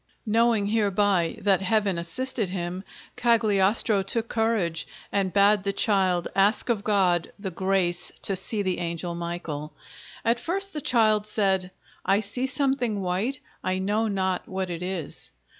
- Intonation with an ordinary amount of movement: Yes, average, 3.3 semitones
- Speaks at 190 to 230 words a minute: No, average, 145 wpm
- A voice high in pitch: Yes, high, 200 Hz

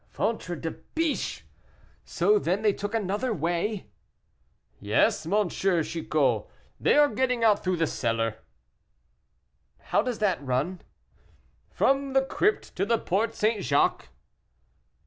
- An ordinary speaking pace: No, slow, 130 wpm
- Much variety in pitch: Yes, wide, 6.0 semitones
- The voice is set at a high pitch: Yes, high, 200 Hz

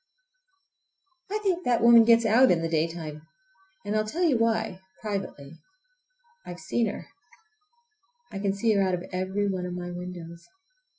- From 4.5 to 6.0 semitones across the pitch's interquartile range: Yes, average, 4.9 semitones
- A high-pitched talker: Yes, high, 205 Hz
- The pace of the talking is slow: No, average, 145 wpm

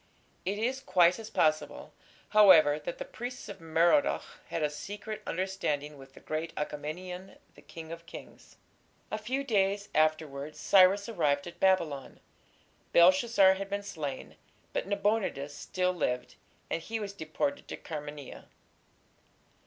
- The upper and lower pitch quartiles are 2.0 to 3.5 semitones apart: No, average, 4.8 semitones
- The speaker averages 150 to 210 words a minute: No, slow, 135 wpm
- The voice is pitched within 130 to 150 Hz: No, medium, 185 Hz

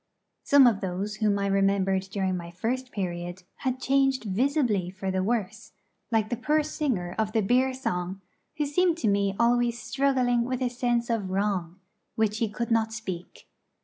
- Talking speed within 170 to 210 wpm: Yes, average, 175 wpm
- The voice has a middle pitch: No, high, 220 Hz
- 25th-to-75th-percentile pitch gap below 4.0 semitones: No, average, 4.6 semitones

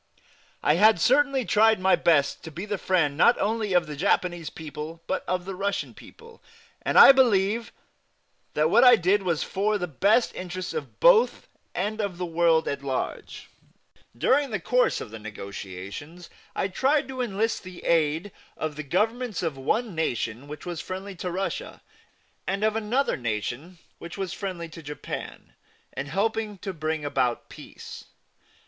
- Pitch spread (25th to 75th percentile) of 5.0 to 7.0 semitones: Yes, wide, 5.5 semitones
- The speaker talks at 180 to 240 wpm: No, average, 165 wpm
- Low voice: No, medium, 185 Hz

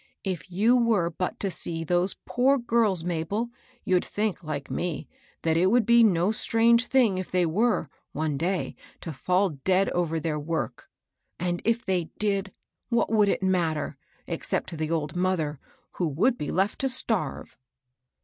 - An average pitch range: Yes, average, 4.9 semitones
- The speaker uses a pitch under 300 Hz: Yes, medium, 185 Hz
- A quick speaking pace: No, average, 170 wpm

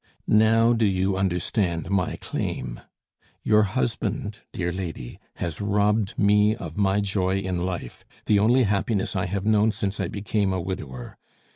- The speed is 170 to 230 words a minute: No, average, 150 wpm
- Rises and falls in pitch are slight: Yes, narrow, 2.3 semitones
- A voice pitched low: Yes, low, 100 Hz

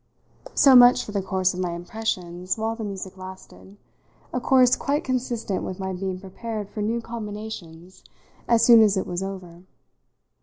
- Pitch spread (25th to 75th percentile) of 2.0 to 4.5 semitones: Yes, average, 3.6 semitones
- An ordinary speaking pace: Yes, average, 165 wpm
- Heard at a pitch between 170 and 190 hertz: No, high, 200 Hz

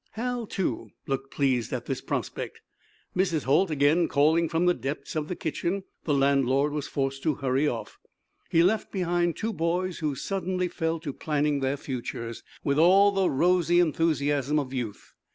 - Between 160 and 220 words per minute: Yes, average, 170 wpm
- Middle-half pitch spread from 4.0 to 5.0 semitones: Yes, average, 4.3 semitones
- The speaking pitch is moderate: Yes, medium, 155 Hz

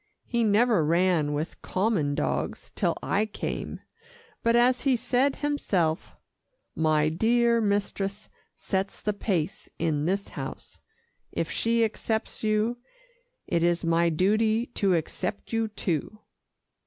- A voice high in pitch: Yes, high, 200 Hz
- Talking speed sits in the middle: No, slow, 125 wpm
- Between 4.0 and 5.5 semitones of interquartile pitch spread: Yes, average, 5.1 semitones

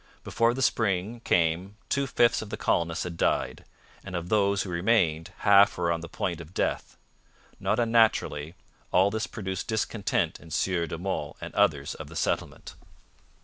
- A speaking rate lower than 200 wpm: Yes, average, 170 wpm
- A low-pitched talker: Yes, very low, 95 Hz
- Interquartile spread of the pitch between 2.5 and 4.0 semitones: No, average, 4.5 semitones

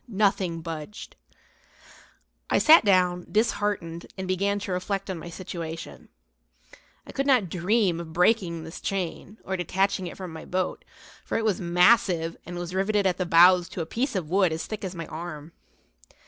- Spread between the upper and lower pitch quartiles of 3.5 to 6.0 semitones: No, average, 2.8 semitones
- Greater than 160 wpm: Yes, average, 175 wpm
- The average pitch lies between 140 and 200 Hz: Yes, medium, 185 Hz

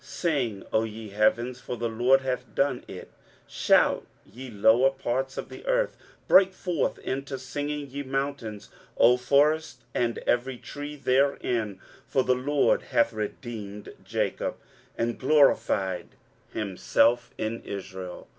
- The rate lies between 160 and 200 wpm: No, slow, 135 wpm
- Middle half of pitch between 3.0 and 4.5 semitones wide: Yes, average, 3.9 semitones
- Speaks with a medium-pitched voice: No, low, 125 Hz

